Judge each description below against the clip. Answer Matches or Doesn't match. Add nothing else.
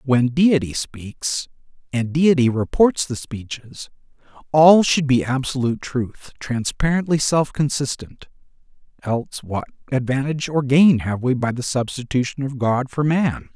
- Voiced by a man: Matches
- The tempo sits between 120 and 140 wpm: Matches